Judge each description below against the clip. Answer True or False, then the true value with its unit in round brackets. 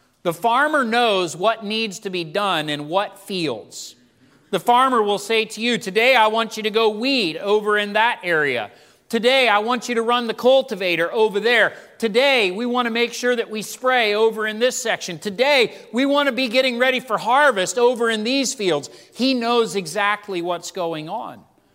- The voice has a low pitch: False (225 Hz)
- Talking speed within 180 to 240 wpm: True (195 wpm)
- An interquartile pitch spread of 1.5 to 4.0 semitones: True (3.7 semitones)